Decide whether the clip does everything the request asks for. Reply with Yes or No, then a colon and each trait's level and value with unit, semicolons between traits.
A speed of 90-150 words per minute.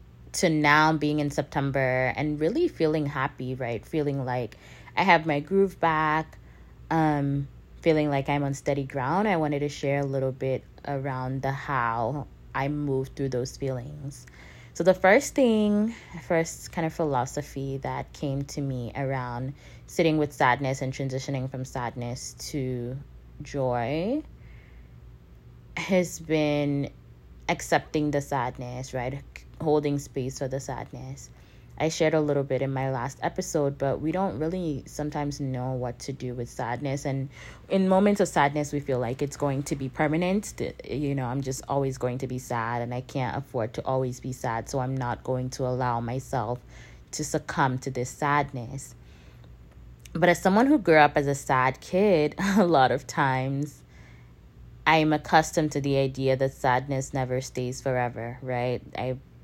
No: average, 165 wpm